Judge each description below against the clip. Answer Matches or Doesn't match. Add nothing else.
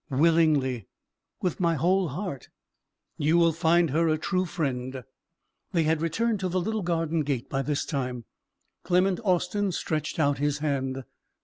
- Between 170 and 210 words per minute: Doesn't match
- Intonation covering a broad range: Doesn't match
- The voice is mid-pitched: Matches